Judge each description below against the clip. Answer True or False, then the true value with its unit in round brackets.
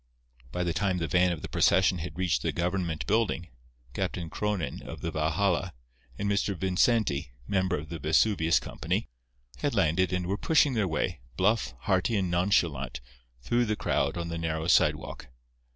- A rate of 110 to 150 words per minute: False (170 wpm)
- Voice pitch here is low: True (90 Hz)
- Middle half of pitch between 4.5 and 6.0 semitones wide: False (3.3 semitones)